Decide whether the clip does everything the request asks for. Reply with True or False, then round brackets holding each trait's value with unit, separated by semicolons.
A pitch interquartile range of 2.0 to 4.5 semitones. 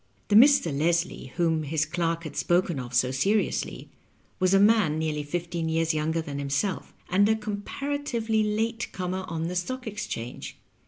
False (5.1 semitones)